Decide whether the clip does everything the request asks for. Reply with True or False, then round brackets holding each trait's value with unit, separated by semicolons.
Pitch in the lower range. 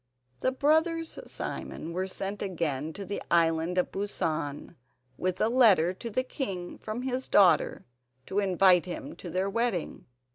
False (190 Hz)